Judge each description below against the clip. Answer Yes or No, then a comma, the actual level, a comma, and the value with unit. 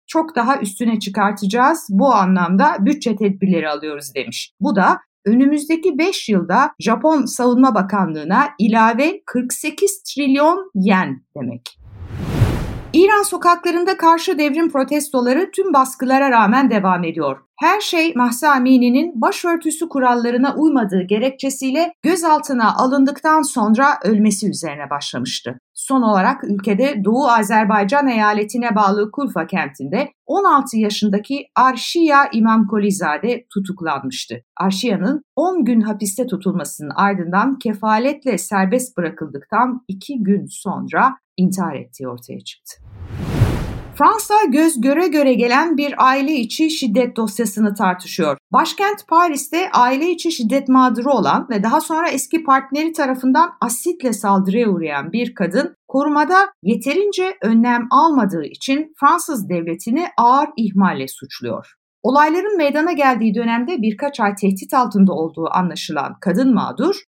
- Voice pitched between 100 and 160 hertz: No, high, 245 Hz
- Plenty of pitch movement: Yes, wide, 6.4 semitones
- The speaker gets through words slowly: No, average, 115 wpm